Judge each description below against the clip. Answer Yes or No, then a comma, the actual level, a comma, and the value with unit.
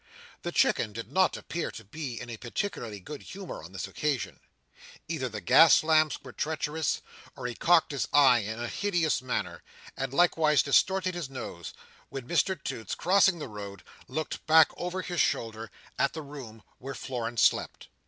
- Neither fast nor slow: Yes, average, 175 wpm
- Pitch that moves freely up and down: Yes, wide, 6.1 semitones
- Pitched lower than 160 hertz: Yes, medium, 140 Hz